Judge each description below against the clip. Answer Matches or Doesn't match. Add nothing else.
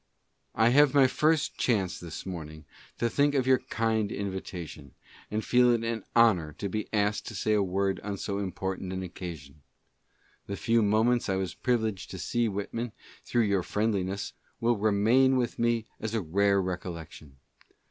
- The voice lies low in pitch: Matches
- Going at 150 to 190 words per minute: Matches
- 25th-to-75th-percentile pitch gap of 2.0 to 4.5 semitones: Matches